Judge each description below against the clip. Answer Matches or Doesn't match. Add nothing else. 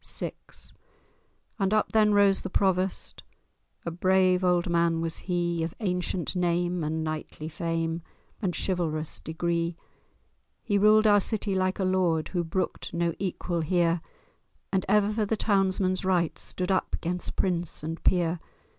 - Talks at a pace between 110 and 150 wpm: Matches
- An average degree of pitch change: Doesn't match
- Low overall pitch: Doesn't match